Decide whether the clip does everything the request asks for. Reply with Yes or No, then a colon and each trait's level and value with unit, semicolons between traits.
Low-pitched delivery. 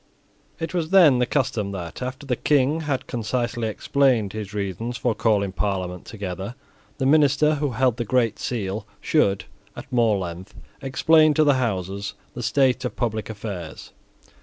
Yes: low, 120 Hz